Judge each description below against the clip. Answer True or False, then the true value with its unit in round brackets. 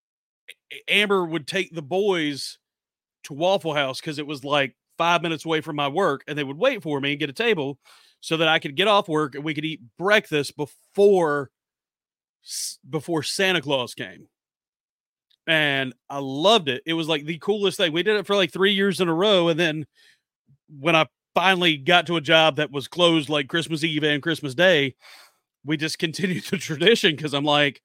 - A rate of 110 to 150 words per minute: False (195 wpm)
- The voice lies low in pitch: False (160 Hz)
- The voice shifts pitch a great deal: False (3.5 semitones)